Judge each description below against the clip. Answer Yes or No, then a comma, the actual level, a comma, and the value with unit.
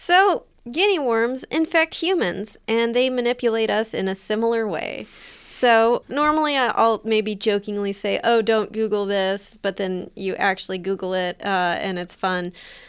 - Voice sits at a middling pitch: No, high, 220 Hz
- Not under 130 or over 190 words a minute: Yes, average, 155 wpm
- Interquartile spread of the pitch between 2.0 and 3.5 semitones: No, average, 3.9 semitones